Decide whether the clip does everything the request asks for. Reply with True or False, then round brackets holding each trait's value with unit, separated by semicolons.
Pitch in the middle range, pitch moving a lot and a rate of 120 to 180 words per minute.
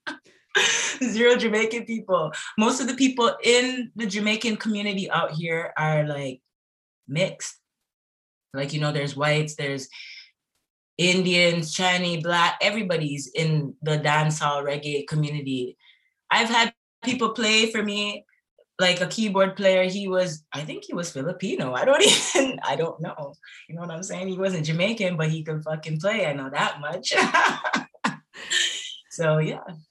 True (180 Hz; 6.1 semitones; 145 wpm)